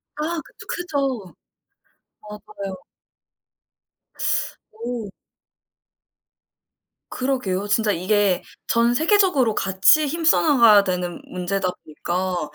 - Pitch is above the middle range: Yes, high, 215 Hz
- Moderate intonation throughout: No, wide, 6.4 semitones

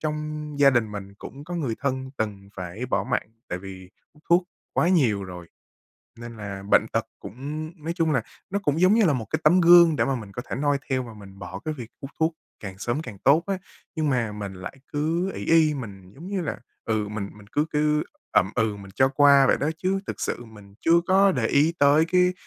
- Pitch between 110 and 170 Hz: Yes, low, 135 Hz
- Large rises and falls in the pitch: Yes, wide, 7.1 semitones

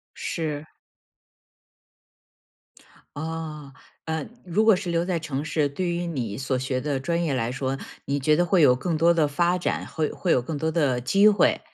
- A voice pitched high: No, medium, 155 Hz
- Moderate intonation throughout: Yes, average, 3.9 semitones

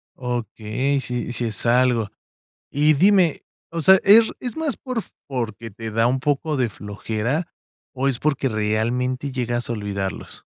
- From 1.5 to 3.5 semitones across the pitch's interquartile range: No, average, 4.6 semitones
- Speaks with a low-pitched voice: Yes, low, 125 Hz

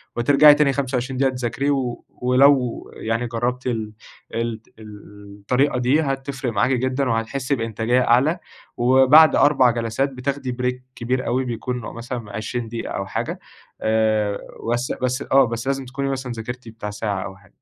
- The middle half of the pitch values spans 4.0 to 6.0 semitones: No, average, 2.7 semitones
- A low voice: Yes, low, 125 Hz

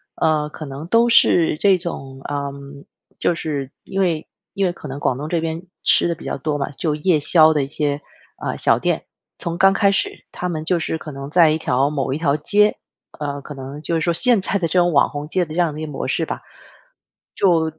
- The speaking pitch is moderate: Yes, medium, 155 Hz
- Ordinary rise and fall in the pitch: Yes, average, 3.3 semitones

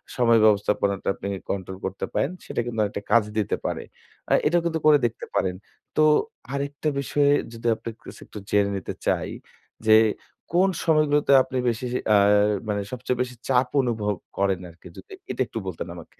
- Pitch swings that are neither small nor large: No, wide, 5.7 semitones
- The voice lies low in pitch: Yes, low, 120 Hz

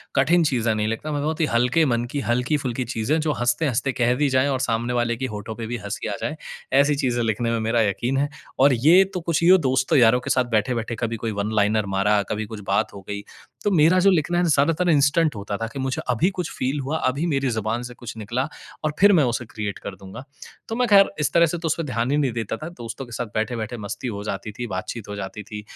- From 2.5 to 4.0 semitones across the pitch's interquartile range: No, average, 4.9 semitones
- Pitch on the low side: Yes, low, 125 Hz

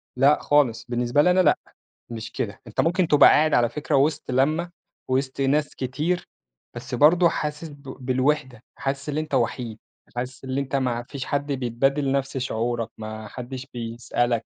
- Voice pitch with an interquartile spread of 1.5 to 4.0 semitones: Yes, average, 3.4 semitones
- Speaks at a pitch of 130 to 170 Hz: Yes, low, 135 Hz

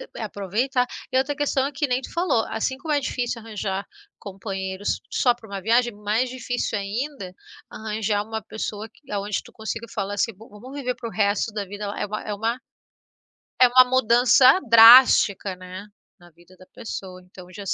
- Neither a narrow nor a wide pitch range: Yes, average, 3.8 semitones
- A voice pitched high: Yes, high, 220 Hz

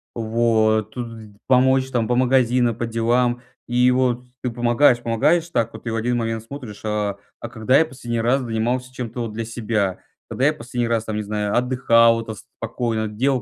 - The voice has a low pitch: Yes, low, 120 Hz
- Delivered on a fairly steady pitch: Yes, narrow, 2.1 semitones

